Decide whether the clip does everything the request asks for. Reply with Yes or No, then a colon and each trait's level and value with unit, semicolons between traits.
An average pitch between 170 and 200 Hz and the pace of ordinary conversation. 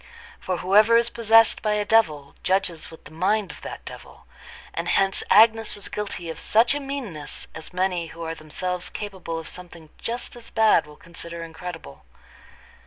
Yes: medium, 185 Hz; average, 175 wpm